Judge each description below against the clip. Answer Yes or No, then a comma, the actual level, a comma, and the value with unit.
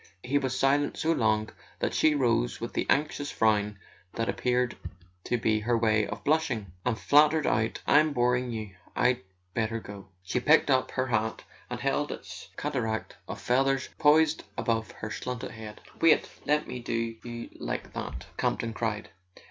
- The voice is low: Yes, low, 120 Hz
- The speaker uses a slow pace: No, average, 160 wpm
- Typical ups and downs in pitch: Yes, average, 3.8 semitones